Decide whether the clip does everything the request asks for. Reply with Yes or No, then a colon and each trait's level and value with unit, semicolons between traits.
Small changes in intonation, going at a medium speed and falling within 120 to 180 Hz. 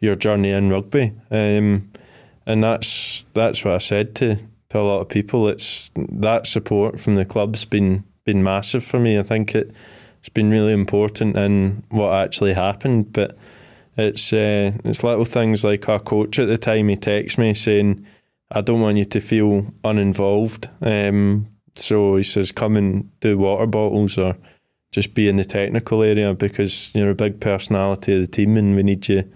No: narrow, 1.7 semitones; average, 185 wpm; low, 105 Hz